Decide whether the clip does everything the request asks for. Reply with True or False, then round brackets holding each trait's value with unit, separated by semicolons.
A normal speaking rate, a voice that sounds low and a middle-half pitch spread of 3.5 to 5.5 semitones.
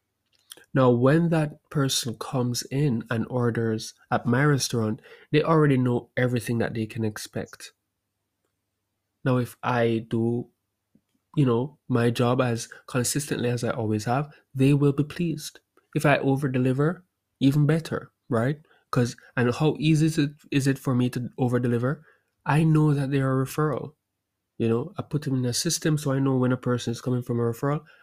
True (175 wpm; 125 Hz; 3.9 semitones)